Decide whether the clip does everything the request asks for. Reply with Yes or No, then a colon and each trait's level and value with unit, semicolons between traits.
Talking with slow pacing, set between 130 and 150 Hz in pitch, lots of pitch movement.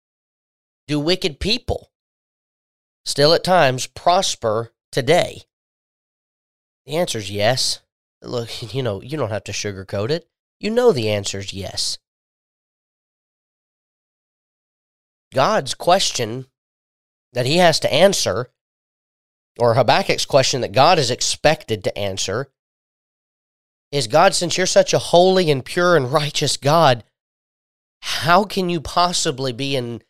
Yes: slow, 120 wpm; medium, 140 Hz; wide, 7.5 semitones